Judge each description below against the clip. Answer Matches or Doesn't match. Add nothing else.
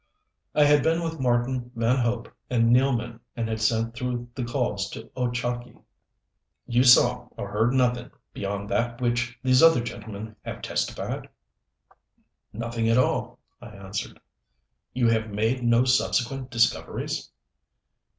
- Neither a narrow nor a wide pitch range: Doesn't match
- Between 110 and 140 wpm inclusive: Matches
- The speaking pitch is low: Matches